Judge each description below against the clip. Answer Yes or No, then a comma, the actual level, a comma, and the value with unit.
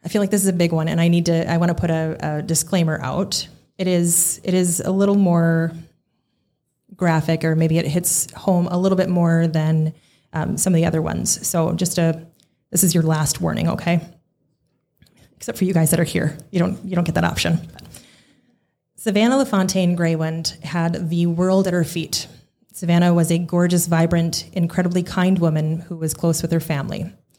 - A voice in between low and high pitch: Yes, medium, 170 Hz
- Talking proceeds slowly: No, average, 195 wpm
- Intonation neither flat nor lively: No, narrow, 2.0 semitones